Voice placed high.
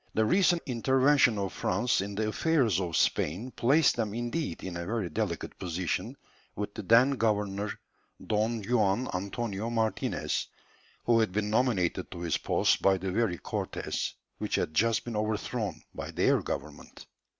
No: low, 110 Hz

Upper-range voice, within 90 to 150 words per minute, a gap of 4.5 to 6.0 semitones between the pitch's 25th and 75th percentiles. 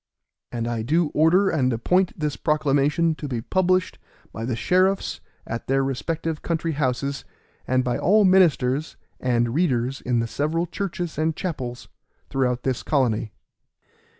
No: medium, 145 Hz; average, 145 wpm; average, 5.1 semitones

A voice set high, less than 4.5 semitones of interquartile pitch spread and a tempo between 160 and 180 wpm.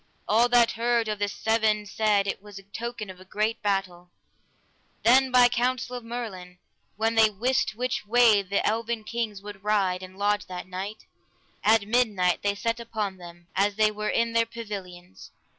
Yes: high, 215 Hz; average, 2.7 semitones; average, 175 wpm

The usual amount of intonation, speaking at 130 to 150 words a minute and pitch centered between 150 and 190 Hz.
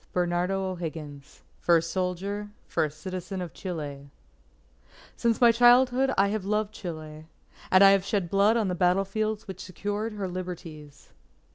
No: average, 3.4 semitones; average, 160 wpm; medium, 185 Hz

